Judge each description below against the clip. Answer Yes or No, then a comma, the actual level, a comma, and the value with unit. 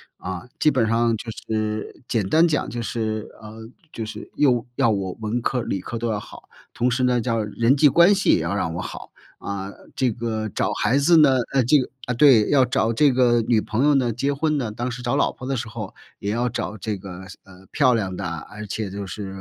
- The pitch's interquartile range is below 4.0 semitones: Yes, average, 3.3 semitones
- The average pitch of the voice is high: No, low, 115 Hz